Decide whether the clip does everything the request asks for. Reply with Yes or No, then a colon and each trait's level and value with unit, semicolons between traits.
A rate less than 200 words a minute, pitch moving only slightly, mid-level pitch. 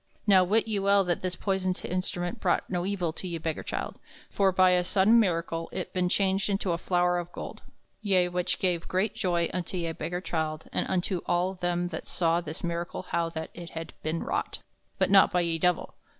No: fast, 205 wpm; narrow, 1.9 semitones; medium, 180 Hz